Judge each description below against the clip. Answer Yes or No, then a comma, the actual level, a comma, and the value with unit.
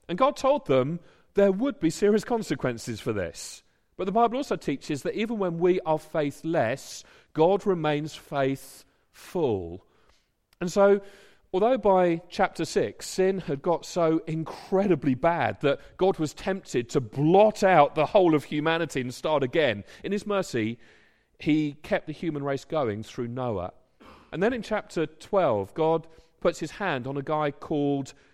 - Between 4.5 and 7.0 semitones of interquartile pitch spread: Yes, average, 5.2 semitones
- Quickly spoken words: No, average, 160 wpm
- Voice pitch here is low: No, medium, 165 Hz